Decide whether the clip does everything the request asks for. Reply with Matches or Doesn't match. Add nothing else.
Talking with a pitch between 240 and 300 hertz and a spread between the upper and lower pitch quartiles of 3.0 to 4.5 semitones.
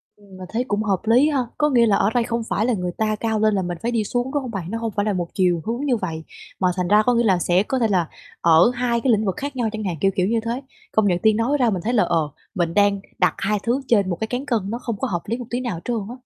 Doesn't match